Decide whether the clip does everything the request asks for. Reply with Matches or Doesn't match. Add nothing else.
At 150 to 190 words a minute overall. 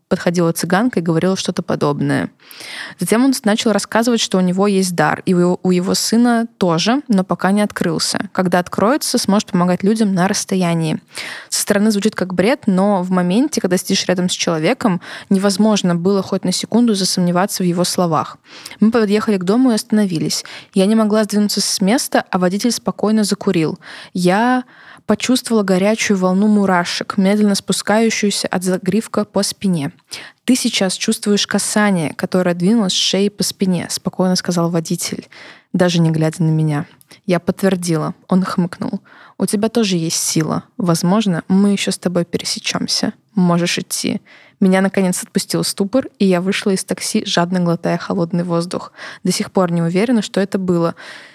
Matches